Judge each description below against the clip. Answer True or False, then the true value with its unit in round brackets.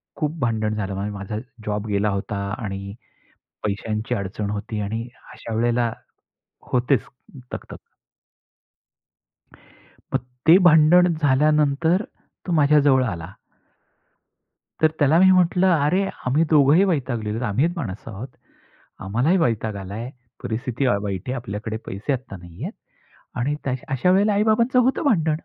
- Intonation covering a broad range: True (6.9 semitones)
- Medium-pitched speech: False (125 Hz)